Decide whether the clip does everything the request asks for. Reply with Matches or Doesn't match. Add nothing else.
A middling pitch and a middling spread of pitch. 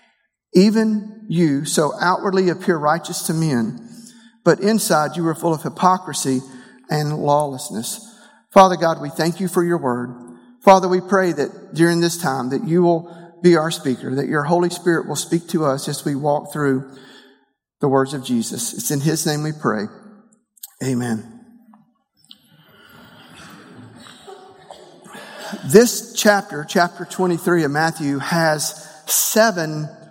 Matches